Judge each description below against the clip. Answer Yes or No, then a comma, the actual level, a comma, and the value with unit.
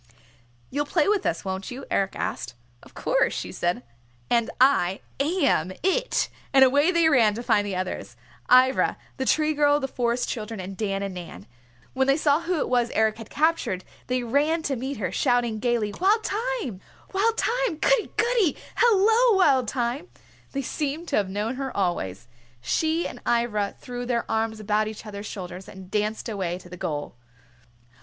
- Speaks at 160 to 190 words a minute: Yes, average, 175 wpm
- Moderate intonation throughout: No, wide, 7.1 semitones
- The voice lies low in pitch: No, high, 245 Hz